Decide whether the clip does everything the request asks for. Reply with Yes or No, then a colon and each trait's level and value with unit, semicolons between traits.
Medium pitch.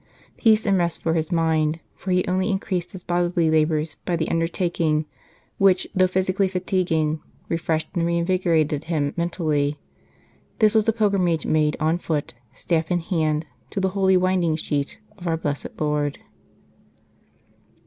Yes: medium, 170 Hz